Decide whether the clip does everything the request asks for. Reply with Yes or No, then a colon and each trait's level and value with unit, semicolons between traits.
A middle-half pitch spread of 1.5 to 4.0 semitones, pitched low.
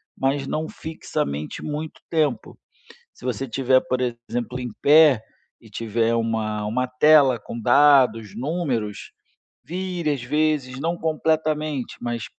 No: average, 4.7 semitones; low, 130 Hz